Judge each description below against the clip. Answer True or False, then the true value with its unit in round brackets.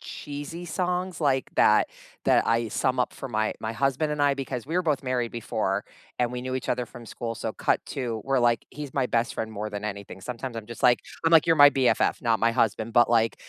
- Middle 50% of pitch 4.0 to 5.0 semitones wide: False (3.6 semitones)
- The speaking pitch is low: True (125 Hz)